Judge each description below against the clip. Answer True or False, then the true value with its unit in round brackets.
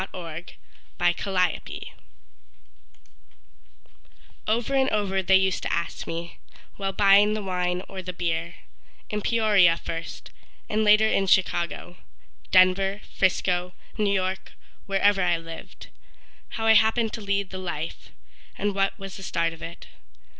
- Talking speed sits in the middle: False (130 wpm)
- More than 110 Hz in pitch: True (190 Hz)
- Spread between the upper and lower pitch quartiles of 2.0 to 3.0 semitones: True (2.7 semitones)